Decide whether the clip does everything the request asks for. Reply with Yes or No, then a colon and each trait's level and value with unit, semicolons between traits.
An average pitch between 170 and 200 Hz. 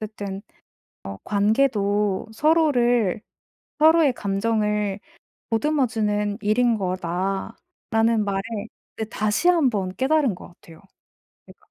No: high, 215 Hz